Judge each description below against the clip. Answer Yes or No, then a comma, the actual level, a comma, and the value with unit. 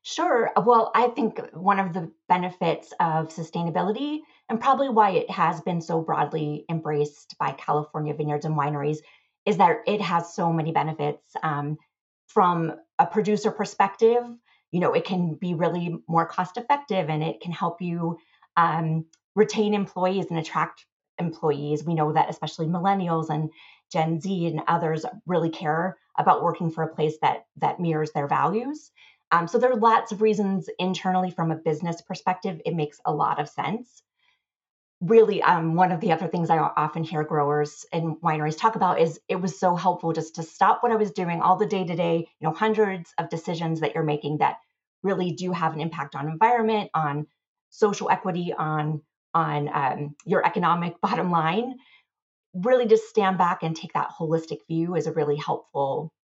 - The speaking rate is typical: Yes, average, 180 wpm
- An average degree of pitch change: Yes, average, 4.0 semitones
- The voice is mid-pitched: Yes, medium, 170 Hz